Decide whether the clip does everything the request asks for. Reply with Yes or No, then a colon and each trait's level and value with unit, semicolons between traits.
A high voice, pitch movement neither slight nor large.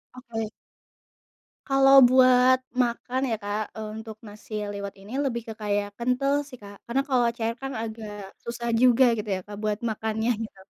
Yes: high, 230 Hz; average, 3.0 semitones